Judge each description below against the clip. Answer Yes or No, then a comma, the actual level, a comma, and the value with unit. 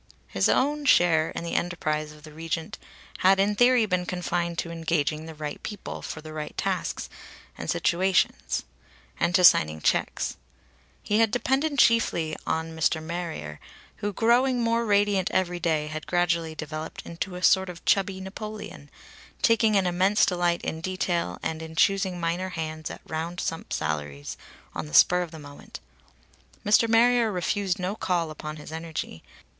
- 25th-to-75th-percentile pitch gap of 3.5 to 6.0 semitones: Yes, average, 3.9 semitones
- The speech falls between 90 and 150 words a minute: No, average, 160 wpm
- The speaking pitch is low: No, medium, 175 Hz